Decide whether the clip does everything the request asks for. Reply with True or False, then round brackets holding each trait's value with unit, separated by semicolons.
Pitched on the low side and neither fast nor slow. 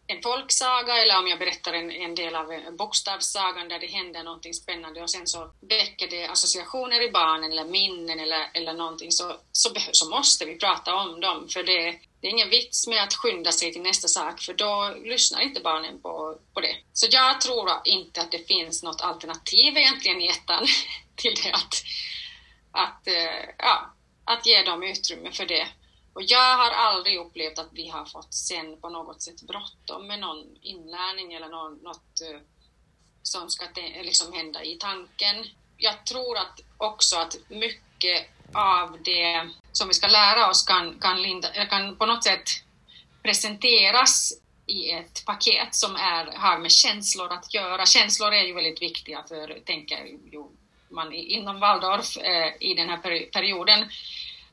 False (180 Hz; 165 wpm)